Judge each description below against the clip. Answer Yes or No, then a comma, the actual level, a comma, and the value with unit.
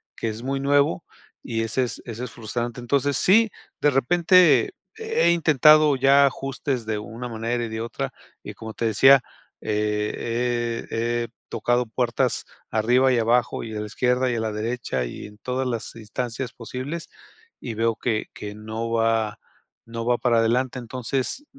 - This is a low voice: Yes, low, 120 Hz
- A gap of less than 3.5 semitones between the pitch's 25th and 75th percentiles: Yes, average, 2.8 semitones